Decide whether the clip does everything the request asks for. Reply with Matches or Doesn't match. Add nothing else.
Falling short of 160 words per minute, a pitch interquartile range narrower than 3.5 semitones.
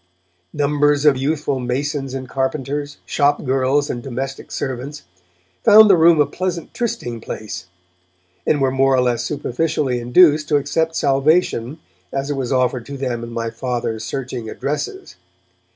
Matches